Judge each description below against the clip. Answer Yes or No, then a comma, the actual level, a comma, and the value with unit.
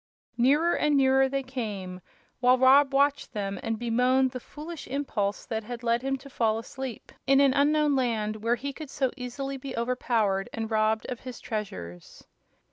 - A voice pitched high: Yes, very high, 250 Hz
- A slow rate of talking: No, average, 175 wpm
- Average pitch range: Yes, average, 3.6 semitones